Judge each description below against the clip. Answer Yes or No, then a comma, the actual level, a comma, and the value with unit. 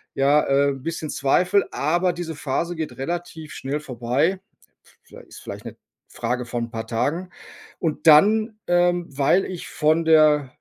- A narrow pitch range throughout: No, average, 4.1 semitones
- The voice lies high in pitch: No, medium, 155 Hz